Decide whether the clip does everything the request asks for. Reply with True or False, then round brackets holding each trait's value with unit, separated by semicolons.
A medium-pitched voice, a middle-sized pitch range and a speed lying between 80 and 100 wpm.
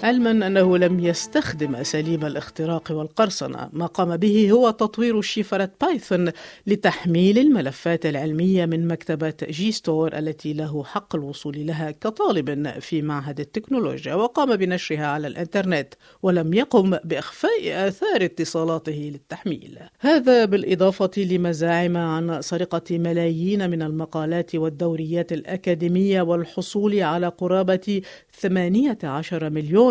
False (175 Hz; 3.7 semitones; 110 wpm)